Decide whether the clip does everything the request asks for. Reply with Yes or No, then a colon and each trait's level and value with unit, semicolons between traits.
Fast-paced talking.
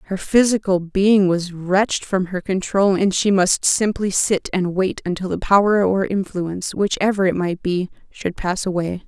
No: average, 180 wpm